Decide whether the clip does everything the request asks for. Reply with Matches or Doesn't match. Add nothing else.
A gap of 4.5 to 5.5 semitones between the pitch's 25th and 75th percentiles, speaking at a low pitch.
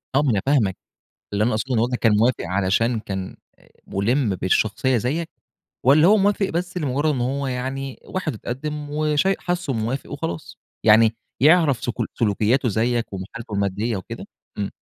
Matches